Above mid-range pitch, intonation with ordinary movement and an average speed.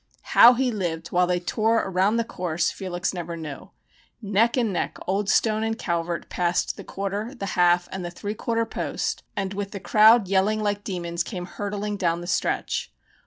Yes: high, 195 Hz; average, 3.5 semitones; average, 185 wpm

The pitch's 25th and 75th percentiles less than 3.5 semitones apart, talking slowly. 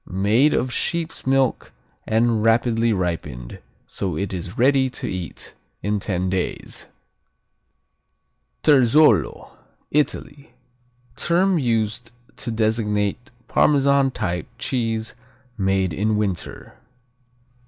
No: average, 5.1 semitones; slow, 95 wpm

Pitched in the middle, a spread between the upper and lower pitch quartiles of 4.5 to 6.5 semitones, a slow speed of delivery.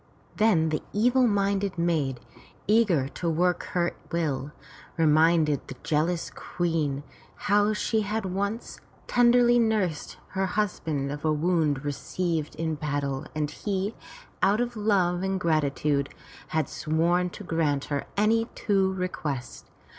Yes: medium, 170 Hz; average, 5.0 semitones; slow, 125 wpm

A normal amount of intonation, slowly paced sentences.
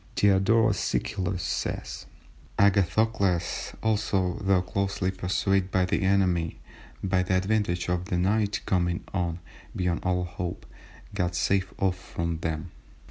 No: narrow, 1.8 semitones; slow, 125 wpm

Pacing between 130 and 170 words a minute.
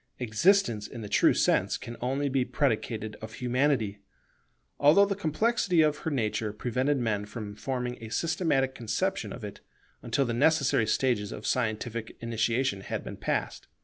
Yes: average, 155 wpm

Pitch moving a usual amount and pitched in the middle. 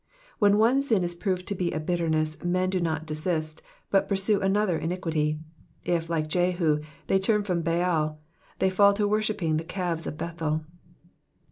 Yes: average, 3.3 semitones; medium, 175 Hz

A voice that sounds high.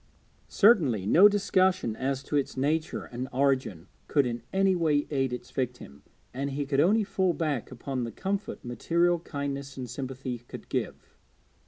No: medium, 140 Hz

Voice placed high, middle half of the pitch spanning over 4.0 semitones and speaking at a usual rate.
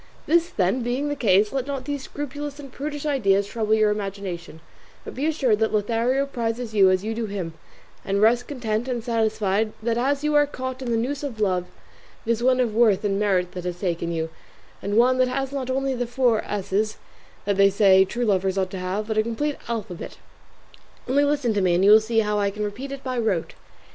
No: high, 225 Hz; average, 4.5 semitones; fast, 220 wpm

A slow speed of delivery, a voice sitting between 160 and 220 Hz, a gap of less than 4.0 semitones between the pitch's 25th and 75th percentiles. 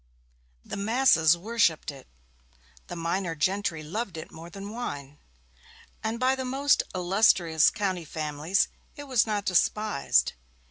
No: slow, 130 wpm; high, 190 Hz; wide, 5.5 semitones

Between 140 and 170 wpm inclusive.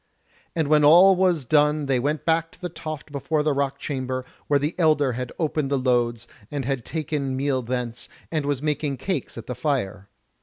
No: average, 195 wpm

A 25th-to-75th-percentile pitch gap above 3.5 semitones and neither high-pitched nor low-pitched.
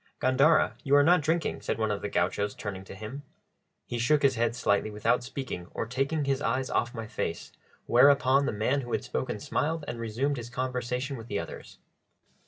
No: average, 4.0 semitones; low, 125 Hz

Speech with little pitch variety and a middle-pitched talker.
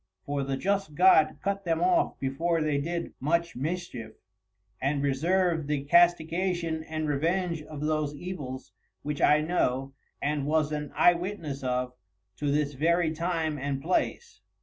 No: average, 3.4 semitones; medium, 155 Hz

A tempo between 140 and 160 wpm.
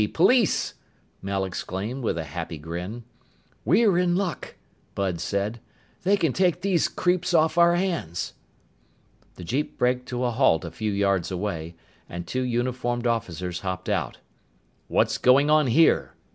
Yes: average, 145 wpm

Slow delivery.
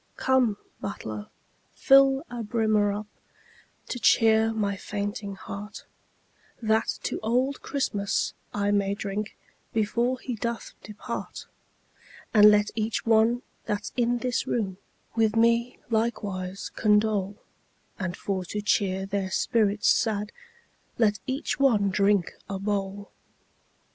Yes: slow, 120 wpm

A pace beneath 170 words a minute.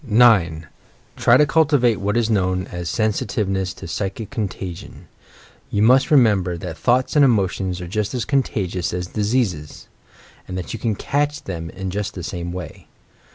Yes: average, 160 wpm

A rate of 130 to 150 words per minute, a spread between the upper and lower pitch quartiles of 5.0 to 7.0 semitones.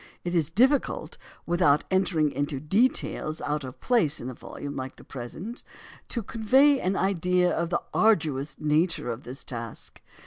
No: average, 160 wpm; wide, 5.4 semitones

